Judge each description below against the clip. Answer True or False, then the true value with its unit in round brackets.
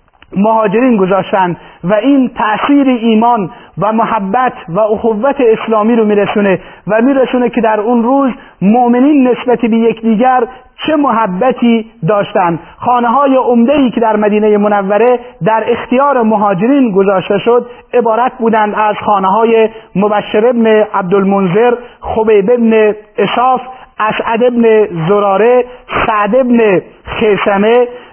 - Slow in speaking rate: False (120 wpm)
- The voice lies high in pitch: True (225 Hz)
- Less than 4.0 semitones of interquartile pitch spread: True (2.7 semitones)